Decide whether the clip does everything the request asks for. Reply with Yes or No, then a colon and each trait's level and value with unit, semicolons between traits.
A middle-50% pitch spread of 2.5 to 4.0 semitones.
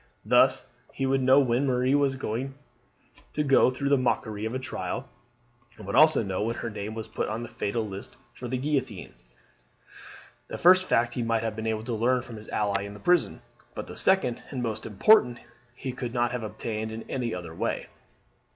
Yes: average, 3.3 semitones